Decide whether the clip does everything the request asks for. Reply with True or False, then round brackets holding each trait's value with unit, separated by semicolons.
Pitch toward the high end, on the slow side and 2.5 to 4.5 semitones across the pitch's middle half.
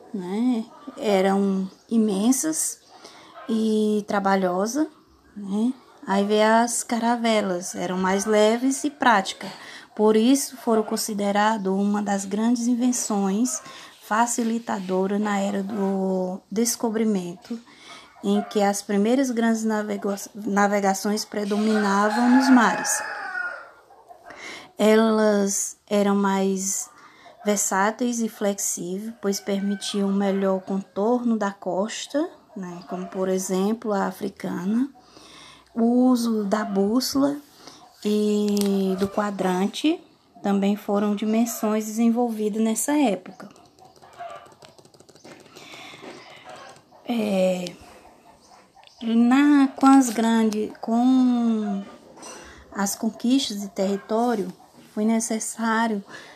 True (215 Hz; 85 wpm; 3.0 semitones)